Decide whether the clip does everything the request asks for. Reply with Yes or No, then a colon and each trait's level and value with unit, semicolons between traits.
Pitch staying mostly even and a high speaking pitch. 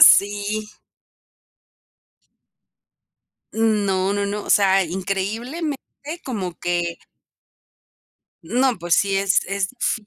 Yes: narrow, 2.3 semitones; high, 200 Hz